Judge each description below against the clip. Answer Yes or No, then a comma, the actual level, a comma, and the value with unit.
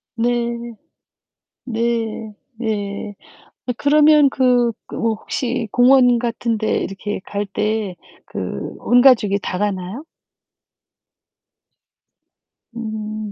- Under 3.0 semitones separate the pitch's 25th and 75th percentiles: Yes, narrow, 2.6 semitones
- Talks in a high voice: Yes, high, 230 Hz